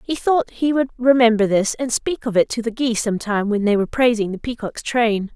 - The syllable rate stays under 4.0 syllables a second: No, 5.5 syllables/s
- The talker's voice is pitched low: No, high, 230 Hz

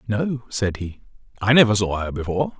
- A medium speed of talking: Yes, average, 185 wpm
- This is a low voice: Yes, low, 110 Hz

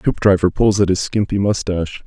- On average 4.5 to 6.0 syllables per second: Yes, 5.4 syllables/s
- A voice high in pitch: No, very low, 95 Hz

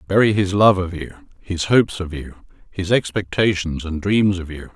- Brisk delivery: No, average, 190 wpm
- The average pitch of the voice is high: No, very low, 90 Hz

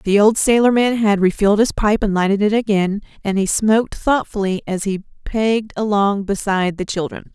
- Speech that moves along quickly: No, average, 180 wpm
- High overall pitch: Yes, high, 205 Hz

